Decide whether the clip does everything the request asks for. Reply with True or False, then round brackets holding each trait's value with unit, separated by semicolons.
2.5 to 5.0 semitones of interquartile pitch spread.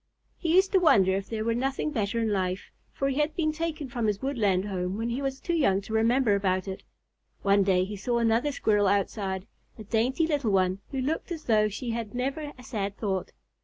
False (5.4 semitones)